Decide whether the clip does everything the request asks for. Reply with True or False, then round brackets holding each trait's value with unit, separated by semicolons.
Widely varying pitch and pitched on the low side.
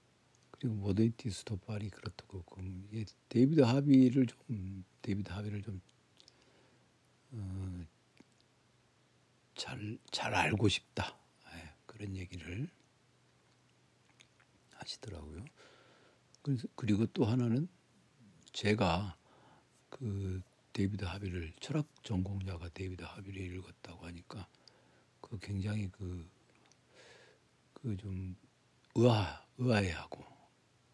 False (3.9 semitones; 100 Hz)